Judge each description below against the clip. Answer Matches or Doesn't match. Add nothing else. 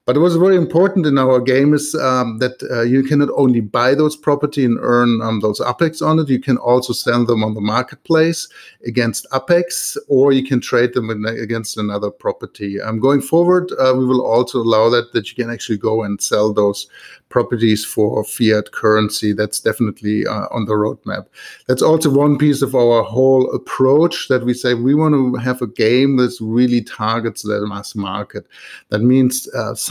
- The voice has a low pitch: Matches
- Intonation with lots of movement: Doesn't match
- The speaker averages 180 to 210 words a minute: Matches